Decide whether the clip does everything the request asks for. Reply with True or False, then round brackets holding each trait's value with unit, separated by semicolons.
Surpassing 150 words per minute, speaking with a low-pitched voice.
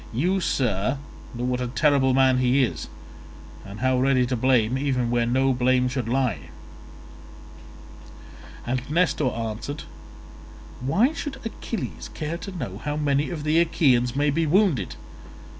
False (140 wpm; 130 Hz)